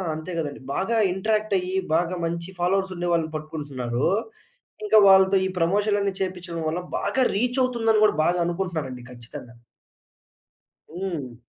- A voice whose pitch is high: No, medium, 180 Hz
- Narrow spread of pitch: No, average, 3.9 semitones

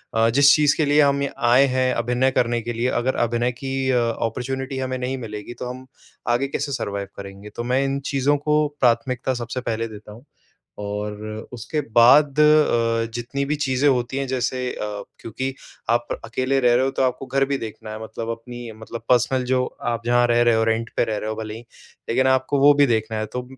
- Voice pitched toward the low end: Yes, low, 125 Hz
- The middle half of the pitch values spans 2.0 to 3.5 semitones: Yes, narrow, 2.5 semitones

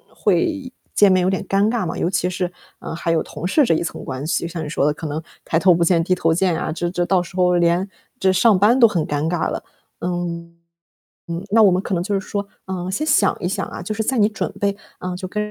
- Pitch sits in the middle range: Yes, medium, 180 Hz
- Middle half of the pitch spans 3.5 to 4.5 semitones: No, average, 3.0 semitones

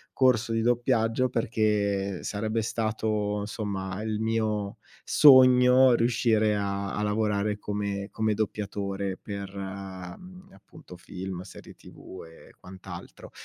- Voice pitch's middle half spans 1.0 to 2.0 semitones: No, narrow, 2.4 semitones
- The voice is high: No, low, 105 Hz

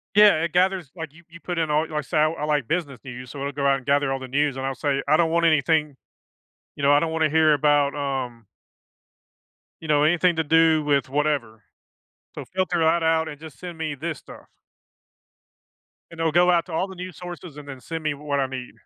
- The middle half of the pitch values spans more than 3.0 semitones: No, average, 2.7 semitones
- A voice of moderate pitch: Yes, medium, 155 Hz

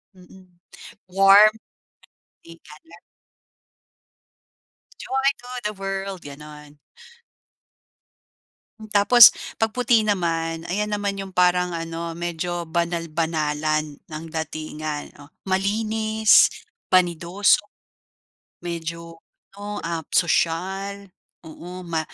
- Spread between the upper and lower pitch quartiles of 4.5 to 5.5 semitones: No, average, 3.3 semitones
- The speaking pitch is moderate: Yes, medium, 175 Hz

